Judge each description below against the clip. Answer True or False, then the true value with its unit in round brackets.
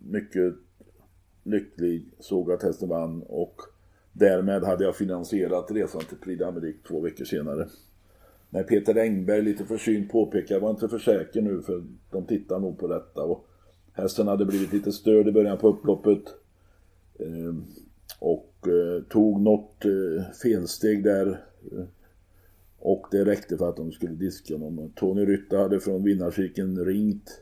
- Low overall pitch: True (95 Hz)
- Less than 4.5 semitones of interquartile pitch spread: True (2.4 semitones)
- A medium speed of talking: True (145 wpm)